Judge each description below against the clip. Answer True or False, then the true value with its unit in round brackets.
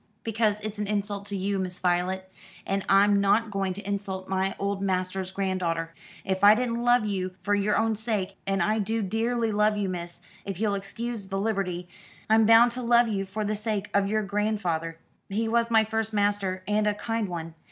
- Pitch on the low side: False (205 Hz)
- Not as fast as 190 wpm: False (200 wpm)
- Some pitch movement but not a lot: False (2.3 semitones)